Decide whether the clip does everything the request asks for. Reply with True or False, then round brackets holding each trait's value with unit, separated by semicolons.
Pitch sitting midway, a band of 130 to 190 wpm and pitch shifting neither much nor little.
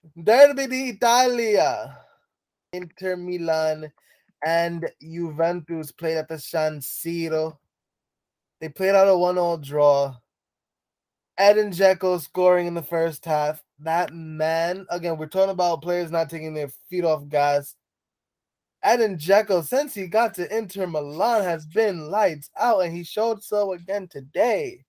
True (170 Hz; 135 wpm; 3.4 semitones)